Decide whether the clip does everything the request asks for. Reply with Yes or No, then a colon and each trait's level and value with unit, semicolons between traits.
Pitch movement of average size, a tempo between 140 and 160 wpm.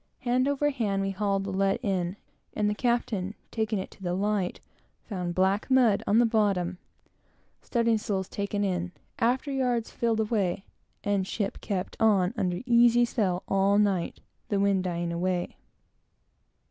Yes: average, 3.4 semitones; average, 150 wpm